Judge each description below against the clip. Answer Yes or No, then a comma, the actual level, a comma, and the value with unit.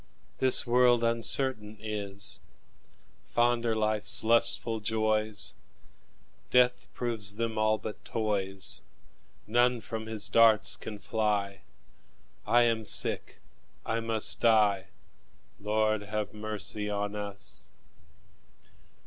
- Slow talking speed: Yes, slow, 100 wpm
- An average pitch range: No, narrow, 1.8 semitones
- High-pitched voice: No, low, 110 Hz